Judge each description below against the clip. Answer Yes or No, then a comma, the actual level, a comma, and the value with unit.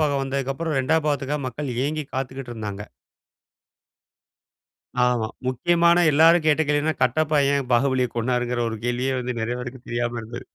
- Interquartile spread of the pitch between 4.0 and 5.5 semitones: No, average, 3.5 semitones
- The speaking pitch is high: No, low, 135 Hz